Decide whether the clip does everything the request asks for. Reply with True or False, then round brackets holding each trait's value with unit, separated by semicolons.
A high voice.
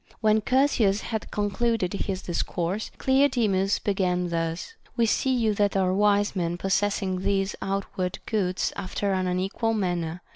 True (195 Hz)